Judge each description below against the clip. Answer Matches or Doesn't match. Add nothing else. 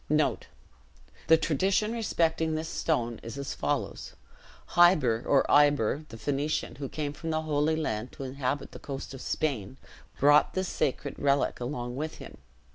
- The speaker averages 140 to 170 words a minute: Matches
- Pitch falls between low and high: Matches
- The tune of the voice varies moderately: Matches